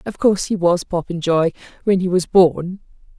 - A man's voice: No, female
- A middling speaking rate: Yes, average, 170 wpm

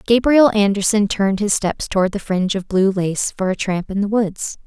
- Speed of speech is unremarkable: No, fast, 220 wpm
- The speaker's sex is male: No, female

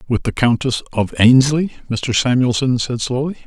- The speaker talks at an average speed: Yes, average, 155 wpm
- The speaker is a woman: No, male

